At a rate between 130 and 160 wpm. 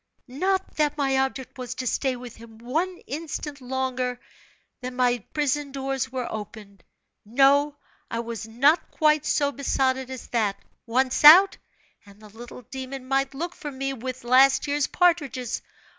Yes: average, 155 wpm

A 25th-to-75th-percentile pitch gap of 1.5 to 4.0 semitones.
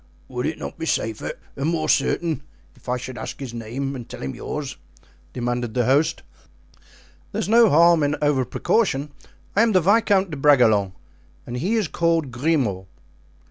No: wide, 5.4 semitones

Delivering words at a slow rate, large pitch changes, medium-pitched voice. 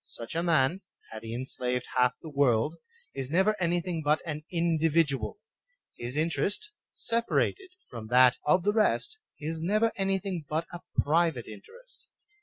No: average, 150 wpm; wide, 6.2 semitones; medium, 160 Hz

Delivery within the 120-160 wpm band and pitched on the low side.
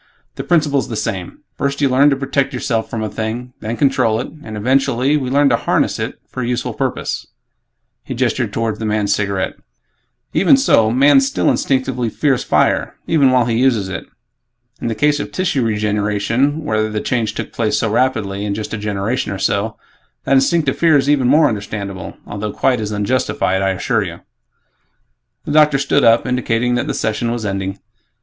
No: average, 185 wpm; low, 120 Hz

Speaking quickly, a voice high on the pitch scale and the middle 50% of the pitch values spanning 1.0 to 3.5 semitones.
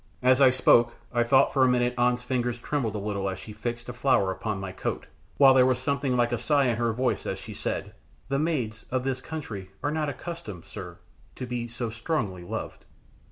No: fast, 215 wpm; low, 125 Hz; average, 3.0 semitones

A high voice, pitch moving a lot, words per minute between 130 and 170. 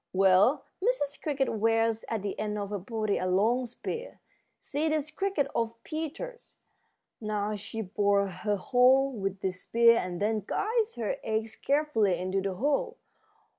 Yes: high, 225 Hz; wide, 5.9 semitones; average, 155 wpm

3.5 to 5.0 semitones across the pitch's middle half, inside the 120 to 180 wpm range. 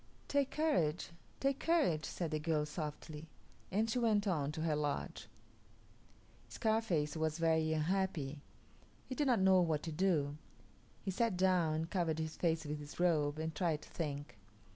Yes: average, 4.0 semitones; average, 165 wpm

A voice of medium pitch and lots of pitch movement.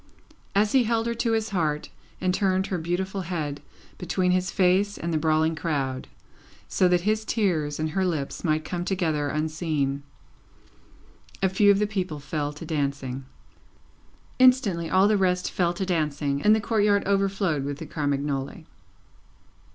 No: medium, 175 Hz; average, 4.6 semitones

